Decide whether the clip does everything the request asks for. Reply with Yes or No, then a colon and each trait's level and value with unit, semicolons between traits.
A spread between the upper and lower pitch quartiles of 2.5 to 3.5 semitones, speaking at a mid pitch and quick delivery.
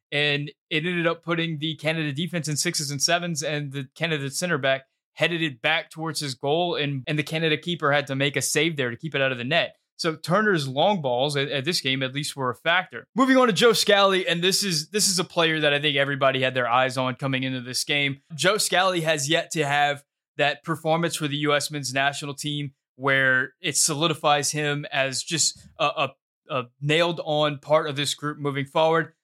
Yes: average, 2.9 semitones; medium, 150 Hz; fast, 225 wpm